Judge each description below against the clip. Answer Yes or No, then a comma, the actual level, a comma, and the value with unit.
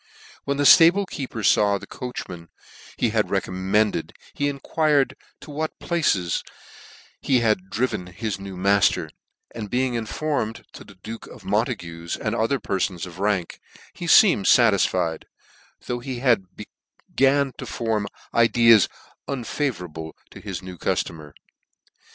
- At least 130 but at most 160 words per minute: Yes, slow, 135 wpm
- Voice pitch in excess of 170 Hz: No, low, 110 Hz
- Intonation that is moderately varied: No, wide, 6.1 semitones